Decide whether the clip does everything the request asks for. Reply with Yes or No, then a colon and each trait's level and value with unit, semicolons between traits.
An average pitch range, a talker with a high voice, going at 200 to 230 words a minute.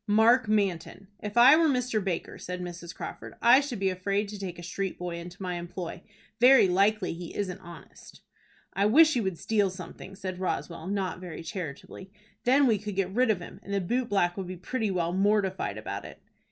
Yes: average, 3.2 semitones; high, 195 Hz; fast, 205 wpm